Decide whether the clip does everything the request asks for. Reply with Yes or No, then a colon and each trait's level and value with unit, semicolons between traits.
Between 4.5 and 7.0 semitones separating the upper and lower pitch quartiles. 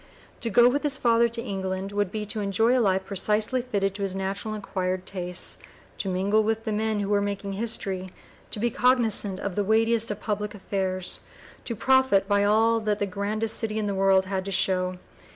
No: narrow, 2.5 semitones